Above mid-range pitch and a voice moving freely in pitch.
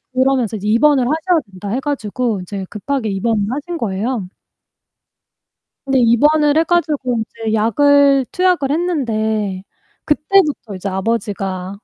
Yes: high, 240 Hz; wide, 5.9 semitones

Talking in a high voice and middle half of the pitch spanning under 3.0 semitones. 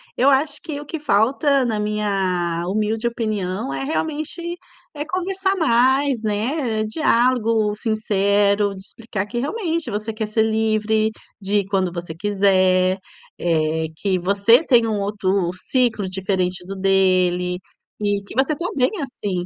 No: high, 215 Hz; average, 4.8 semitones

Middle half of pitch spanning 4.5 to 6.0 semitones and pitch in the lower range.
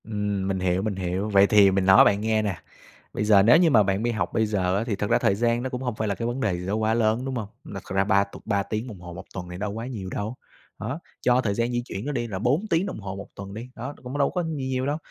No: average, 3.7 semitones; low, 110 Hz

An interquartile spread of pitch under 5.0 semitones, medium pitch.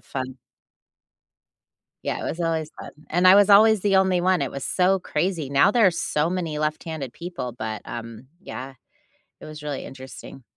No: wide, 5.6 semitones; medium, 160 Hz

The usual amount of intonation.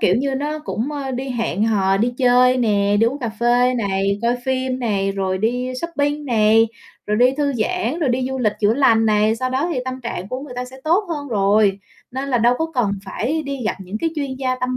Yes: average, 3.9 semitones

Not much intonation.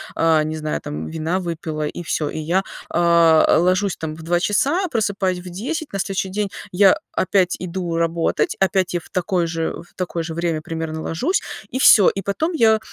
No: average, 3.2 semitones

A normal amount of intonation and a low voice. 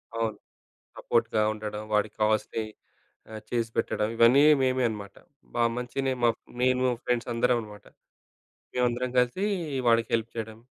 No: narrow, 2.2 semitones; low, 115 Hz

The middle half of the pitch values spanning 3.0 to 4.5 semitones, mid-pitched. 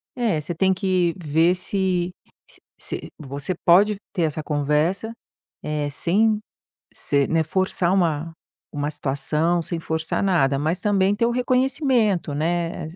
Yes: average, 4.2 semitones; medium, 175 Hz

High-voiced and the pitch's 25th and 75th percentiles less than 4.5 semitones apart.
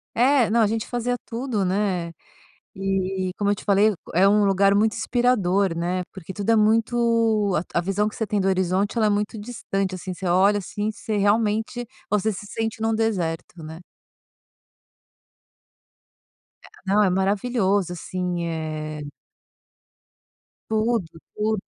Yes: high, 205 Hz; average, 2.9 semitones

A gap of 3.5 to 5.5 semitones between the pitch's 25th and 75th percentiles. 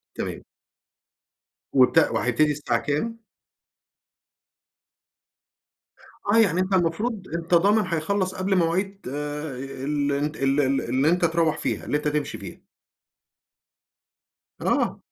Yes: average, 4.6 semitones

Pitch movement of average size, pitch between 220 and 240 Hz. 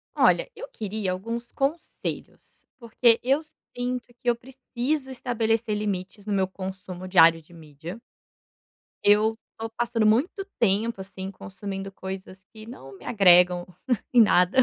No: average, 4.2 semitones; high, 210 Hz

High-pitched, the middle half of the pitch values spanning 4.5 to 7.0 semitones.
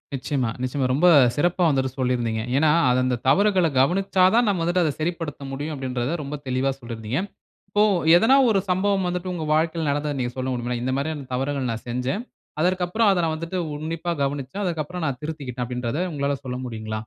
No: medium, 145 Hz; wide, 5.5 semitones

